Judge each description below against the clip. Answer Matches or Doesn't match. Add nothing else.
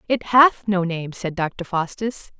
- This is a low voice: Doesn't match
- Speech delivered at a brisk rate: Doesn't match